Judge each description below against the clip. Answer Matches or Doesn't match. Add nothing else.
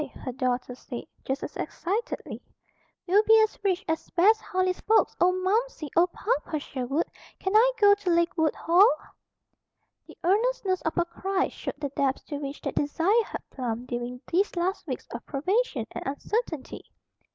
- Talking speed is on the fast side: Doesn't match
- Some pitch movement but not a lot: Doesn't match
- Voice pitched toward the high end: Matches